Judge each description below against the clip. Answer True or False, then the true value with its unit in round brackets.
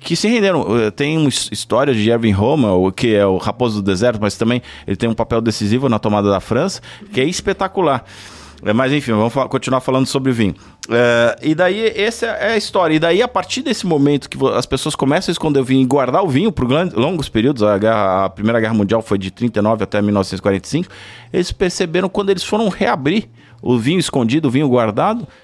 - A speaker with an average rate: False (205 wpm)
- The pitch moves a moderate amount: False (6.6 semitones)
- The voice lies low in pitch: True (125 Hz)